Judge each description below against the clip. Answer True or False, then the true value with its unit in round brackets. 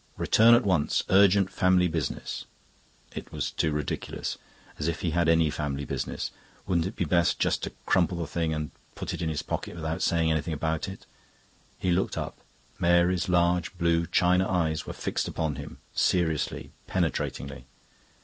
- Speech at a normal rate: True (170 wpm)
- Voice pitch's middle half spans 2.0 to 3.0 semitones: True (2.4 semitones)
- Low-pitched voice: True (85 Hz)